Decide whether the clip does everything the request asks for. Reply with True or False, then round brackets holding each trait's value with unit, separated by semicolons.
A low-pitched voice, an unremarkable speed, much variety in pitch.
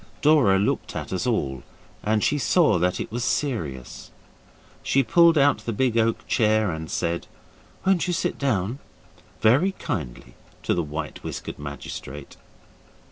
True (110 Hz; 145 wpm; 8.7 semitones)